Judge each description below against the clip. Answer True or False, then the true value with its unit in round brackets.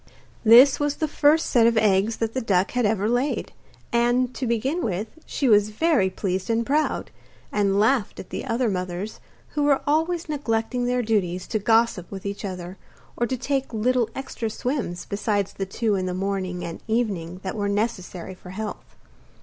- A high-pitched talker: True (220 Hz)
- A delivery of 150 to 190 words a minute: True (180 wpm)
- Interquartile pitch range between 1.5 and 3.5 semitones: False (4.4 semitones)